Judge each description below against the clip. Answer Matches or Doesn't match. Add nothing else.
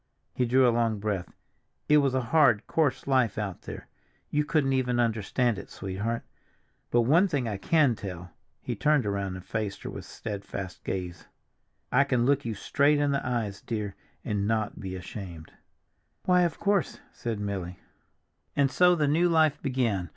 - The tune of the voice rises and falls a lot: Matches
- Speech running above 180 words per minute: Doesn't match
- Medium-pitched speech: Doesn't match